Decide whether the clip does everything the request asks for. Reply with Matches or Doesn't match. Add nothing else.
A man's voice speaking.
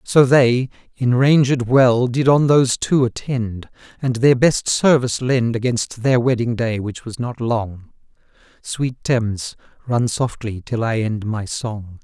Matches